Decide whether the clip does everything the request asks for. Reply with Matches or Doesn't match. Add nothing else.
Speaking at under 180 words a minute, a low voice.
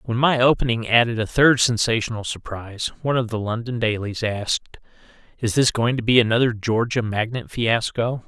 Matches